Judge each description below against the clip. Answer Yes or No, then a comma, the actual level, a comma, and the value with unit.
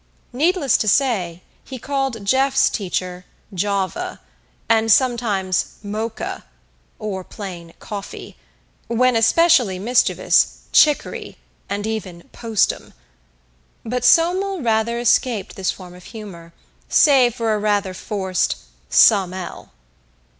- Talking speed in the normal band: No, slow, 105 wpm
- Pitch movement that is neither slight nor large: Yes, average, 4.9 semitones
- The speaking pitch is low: No, high, 220 Hz